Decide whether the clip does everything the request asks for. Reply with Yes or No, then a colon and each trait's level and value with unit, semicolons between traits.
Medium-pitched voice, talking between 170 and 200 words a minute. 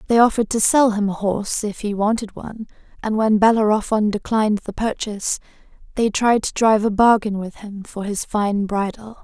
No: high, 210 Hz; average, 190 wpm